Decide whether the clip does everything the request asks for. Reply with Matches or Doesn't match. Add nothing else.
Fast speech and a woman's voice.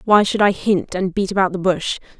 Matches